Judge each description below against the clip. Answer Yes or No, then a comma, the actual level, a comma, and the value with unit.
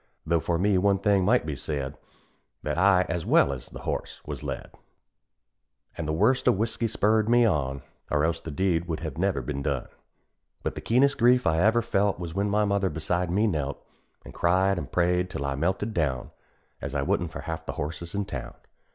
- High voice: No, very low, 90 Hz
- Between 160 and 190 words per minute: No, fast, 205 wpm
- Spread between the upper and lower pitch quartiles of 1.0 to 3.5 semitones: No, average, 4.8 semitones